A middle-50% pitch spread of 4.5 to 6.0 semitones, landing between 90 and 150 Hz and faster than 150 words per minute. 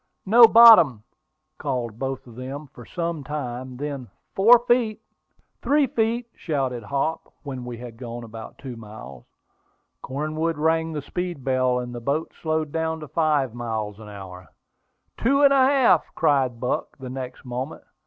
Yes: average, 5.0 semitones; medium, 140 Hz; average, 160 wpm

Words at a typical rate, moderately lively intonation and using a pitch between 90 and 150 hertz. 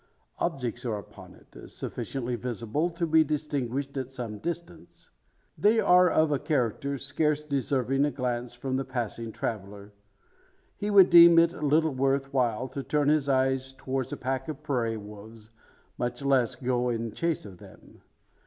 Yes: average, 160 wpm; average, 3.9 semitones; low, 135 Hz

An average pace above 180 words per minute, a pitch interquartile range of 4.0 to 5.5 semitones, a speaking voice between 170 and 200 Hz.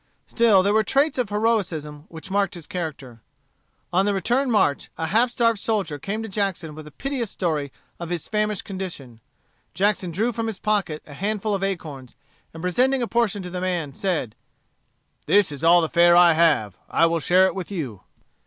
Yes: average, 190 wpm; average, 4.7 semitones; medium, 185 Hz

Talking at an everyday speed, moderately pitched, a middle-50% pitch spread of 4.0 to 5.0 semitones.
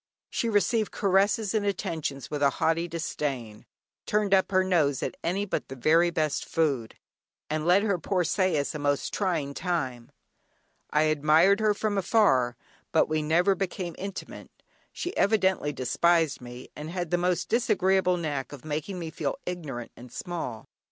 Yes: average, 160 wpm; medium, 170 Hz; average, 4.7 semitones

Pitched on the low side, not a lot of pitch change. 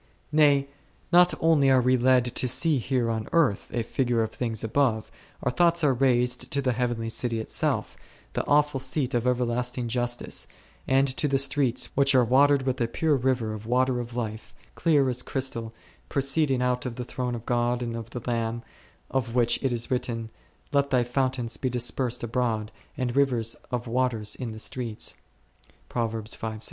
Yes: low, 125 Hz; narrow, 2.3 semitones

